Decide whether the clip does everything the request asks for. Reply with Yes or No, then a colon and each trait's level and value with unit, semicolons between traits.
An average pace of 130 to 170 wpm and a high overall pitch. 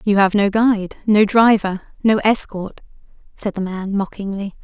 Yes: average, 155 wpm; high, 205 Hz